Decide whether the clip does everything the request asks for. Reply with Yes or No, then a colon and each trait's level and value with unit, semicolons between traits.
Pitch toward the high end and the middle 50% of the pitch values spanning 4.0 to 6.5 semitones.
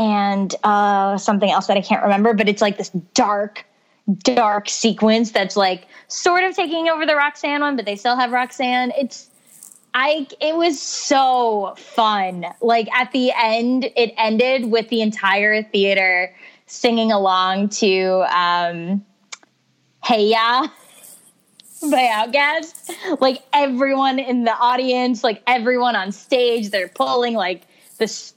Yes: high, 230 Hz; average, 4.3 semitones